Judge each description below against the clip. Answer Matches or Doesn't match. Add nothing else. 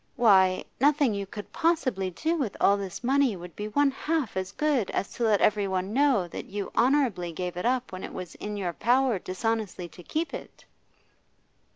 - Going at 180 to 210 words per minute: Matches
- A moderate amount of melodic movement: Doesn't match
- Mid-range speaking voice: Doesn't match